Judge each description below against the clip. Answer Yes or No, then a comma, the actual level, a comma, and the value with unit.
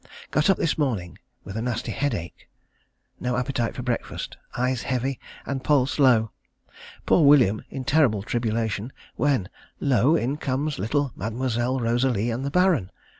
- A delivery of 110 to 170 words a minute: Yes, average, 145 wpm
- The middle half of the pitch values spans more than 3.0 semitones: Yes, average, 3.5 semitones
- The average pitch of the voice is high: No, low, 125 Hz